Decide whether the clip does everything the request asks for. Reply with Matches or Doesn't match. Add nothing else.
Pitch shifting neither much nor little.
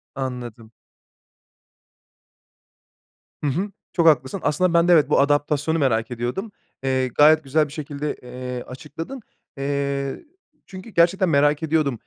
Matches